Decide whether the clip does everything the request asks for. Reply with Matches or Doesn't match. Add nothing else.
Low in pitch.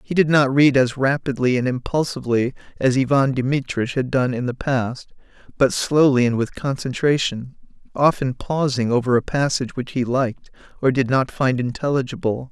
Matches